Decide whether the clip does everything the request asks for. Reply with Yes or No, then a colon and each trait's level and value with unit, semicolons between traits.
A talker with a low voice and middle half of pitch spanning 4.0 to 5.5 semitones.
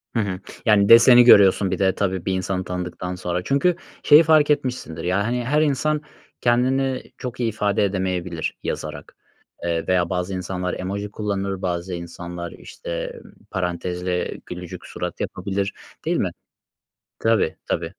Yes: very low, 95 Hz; average, 5.2 semitones